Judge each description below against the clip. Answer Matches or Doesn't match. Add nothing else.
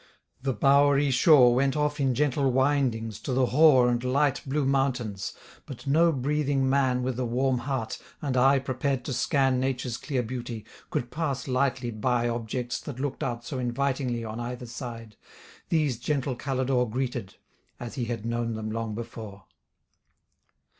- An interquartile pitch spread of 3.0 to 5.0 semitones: Doesn't match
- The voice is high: Doesn't match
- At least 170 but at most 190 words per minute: Doesn't match